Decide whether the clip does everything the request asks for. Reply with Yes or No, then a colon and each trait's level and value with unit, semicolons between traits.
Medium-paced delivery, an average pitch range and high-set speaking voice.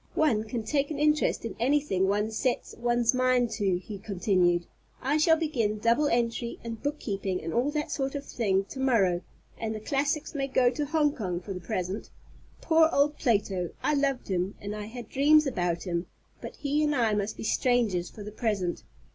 No: average, 195 wpm; wide, 5.9 semitones; high, 230 Hz